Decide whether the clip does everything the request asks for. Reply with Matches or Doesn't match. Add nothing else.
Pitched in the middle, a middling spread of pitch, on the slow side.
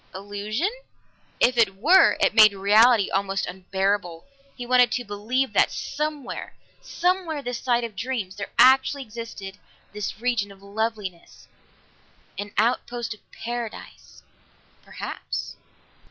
Doesn't match